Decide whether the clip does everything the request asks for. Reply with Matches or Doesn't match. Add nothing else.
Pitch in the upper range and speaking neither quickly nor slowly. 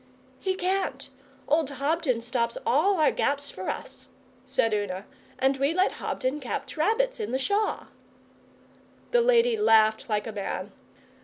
Matches